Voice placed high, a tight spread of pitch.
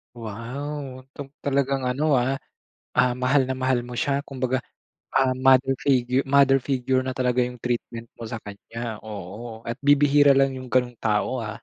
No: low, 130 Hz; narrow, 2.1 semitones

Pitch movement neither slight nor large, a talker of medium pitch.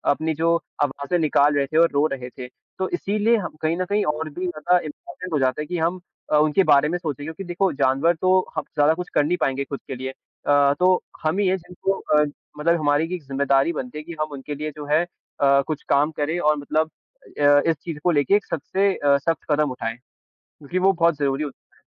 Yes: average, 3.5 semitones; medium, 155 Hz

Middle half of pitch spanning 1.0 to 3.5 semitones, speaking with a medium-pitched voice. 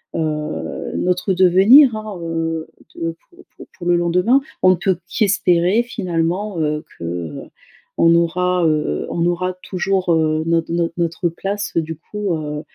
Yes: narrow, 2.5 semitones; medium, 175 Hz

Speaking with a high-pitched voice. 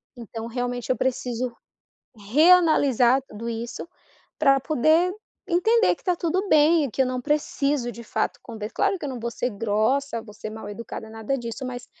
Yes: very high, 250 Hz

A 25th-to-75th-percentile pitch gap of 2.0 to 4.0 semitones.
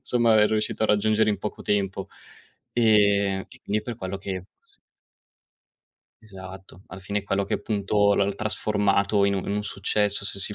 No: narrow, 1.5 semitones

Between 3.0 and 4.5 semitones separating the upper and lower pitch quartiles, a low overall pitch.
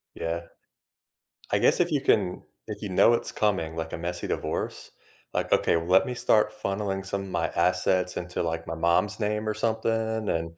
Yes: average, 4.0 semitones; very low, 95 Hz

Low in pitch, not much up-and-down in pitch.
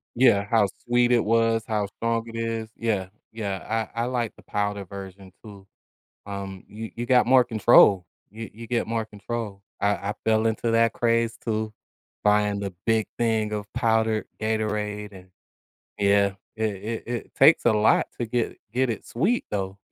Yes: low, 110 Hz; narrow, 2.2 semitones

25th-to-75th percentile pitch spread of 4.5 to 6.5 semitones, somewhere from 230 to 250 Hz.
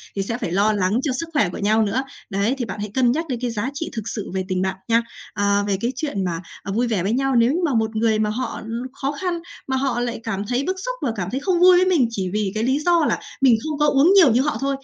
Yes: average, 5.0 semitones; high, 235 Hz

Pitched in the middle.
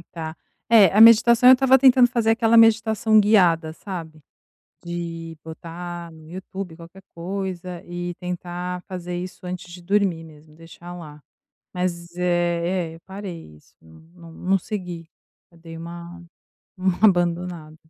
Yes: medium, 175 Hz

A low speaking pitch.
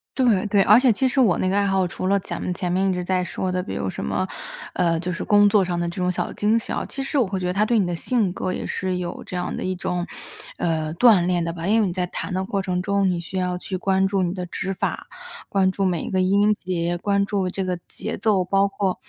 No: medium, 185 Hz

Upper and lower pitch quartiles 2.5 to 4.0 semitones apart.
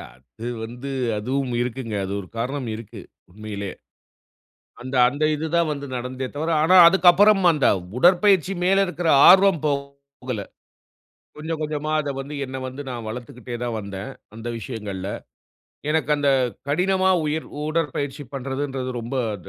No: average, 4.9 semitones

